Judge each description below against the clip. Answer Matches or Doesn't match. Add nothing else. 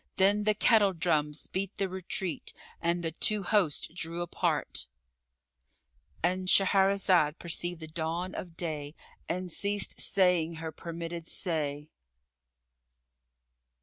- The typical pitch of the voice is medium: Matches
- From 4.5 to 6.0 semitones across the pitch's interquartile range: Doesn't match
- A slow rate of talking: Matches